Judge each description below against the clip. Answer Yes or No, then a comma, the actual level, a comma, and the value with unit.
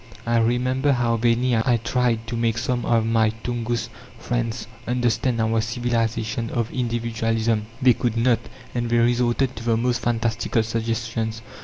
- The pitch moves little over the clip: Yes, narrow, 1.2 semitones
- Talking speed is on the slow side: No, average, 150 wpm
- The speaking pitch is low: Yes, low, 115 Hz